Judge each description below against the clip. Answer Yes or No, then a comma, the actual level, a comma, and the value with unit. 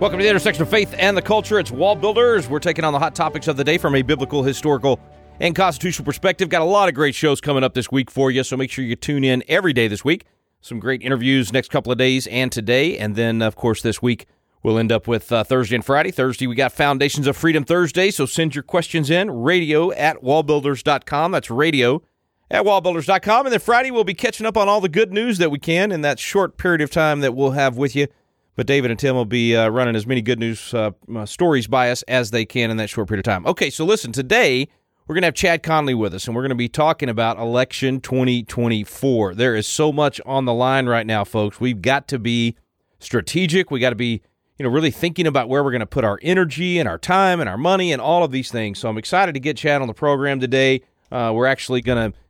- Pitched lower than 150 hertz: Yes, low, 135 Hz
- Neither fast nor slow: No, fast, 255 wpm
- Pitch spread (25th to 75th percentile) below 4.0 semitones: No, average, 5.2 semitones